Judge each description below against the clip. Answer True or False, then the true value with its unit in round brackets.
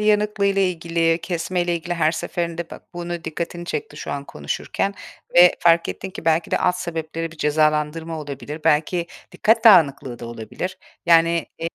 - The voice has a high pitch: False (165 Hz)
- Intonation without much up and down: True (2.2 semitones)